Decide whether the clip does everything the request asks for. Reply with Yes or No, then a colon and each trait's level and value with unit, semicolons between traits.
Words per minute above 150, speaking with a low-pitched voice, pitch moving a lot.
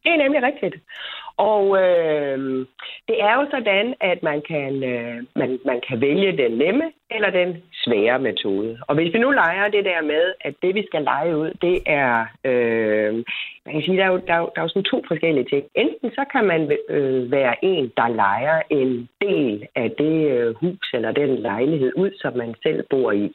No: average, 200 wpm; medium, 160 Hz; wide, 7.4 semitones